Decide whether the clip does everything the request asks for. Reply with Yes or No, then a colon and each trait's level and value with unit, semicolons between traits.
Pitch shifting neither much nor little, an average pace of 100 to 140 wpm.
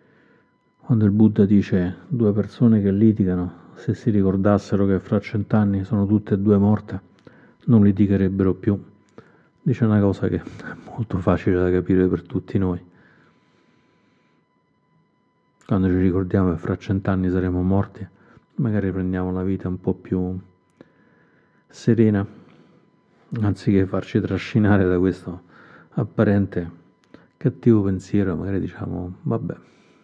No: narrow, 2.2 semitones; average, 120 wpm